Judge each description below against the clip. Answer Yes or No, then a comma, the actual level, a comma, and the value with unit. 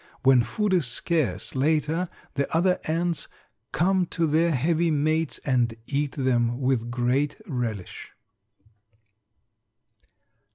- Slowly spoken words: Yes, slow, 110 wpm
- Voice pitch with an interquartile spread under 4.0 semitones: No, average, 5.0 semitones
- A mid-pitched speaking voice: Yes, medium, 145 Hz